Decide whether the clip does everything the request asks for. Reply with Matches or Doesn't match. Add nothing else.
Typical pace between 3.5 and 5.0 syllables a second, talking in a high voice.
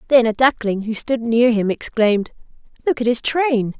Matches